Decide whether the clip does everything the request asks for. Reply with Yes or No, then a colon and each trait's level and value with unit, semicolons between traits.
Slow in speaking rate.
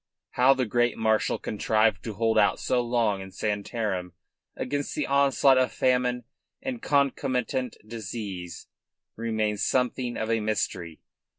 Yes: slow, 130 wpm